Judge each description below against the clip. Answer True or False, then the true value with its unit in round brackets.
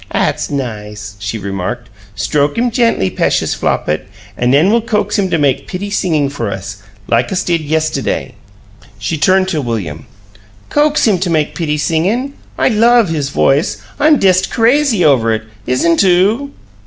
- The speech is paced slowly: False (160 wpm)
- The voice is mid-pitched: True (160 Hz)